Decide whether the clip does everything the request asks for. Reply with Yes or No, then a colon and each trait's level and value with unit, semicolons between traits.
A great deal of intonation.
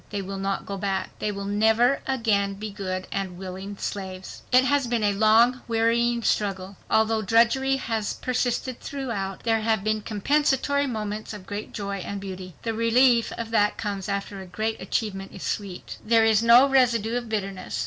No: average, 3.0 semitones